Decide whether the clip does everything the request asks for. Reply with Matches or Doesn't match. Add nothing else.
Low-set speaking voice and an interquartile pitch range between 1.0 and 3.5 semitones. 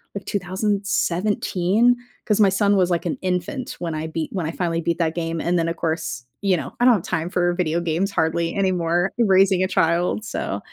Doesn't match